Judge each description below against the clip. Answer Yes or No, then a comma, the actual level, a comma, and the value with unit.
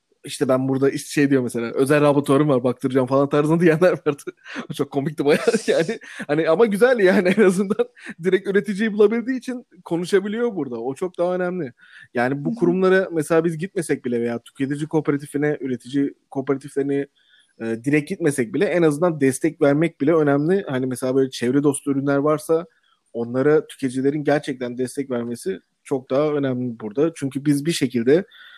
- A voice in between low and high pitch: Yes, medium, 145 Hz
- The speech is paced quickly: Yes, fast, 165 wpm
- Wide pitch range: No, average, 4.7 semitones